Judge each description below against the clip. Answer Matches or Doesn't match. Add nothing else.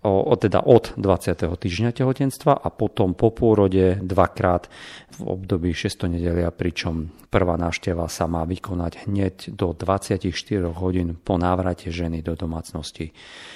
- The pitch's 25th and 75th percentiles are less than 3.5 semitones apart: Matches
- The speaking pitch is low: Matches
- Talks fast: Doesn't match